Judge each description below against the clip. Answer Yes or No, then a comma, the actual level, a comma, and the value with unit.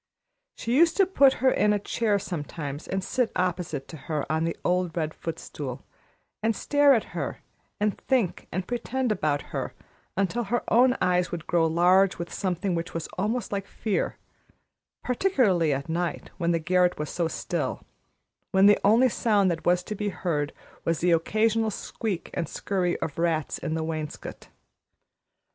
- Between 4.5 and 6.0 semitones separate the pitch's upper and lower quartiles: Yes, average, 4.8 semitones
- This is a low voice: No, medium, 180 Hz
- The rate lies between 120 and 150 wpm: No, average, 170 wpm